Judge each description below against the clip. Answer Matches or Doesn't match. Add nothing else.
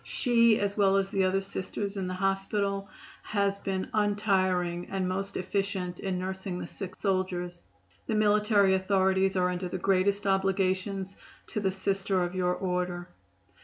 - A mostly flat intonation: Matches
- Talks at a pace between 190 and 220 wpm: Doesn't match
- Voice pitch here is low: Doesn't match